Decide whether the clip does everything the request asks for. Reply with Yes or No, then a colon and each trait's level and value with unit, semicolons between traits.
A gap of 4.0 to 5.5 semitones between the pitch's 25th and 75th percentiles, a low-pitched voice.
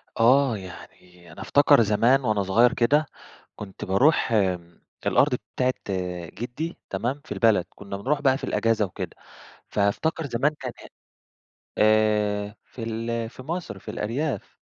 Yes: average, 4.5 semitones; low, 115 Hz